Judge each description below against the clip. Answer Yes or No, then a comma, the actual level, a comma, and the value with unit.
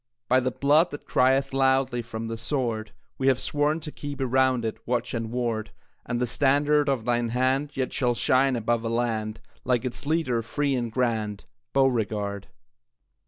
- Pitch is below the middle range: Yes, low, 125 Hz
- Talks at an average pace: Yes, average, 170 wpm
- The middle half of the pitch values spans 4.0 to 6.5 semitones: No, average, 2.9 semitones